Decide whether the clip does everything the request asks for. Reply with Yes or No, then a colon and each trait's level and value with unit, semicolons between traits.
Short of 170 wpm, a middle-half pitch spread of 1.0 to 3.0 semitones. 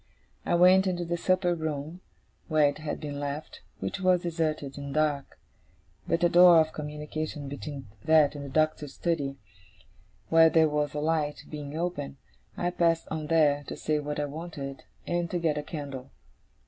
No: average, 175 wpm; narrow, 2.5 semitones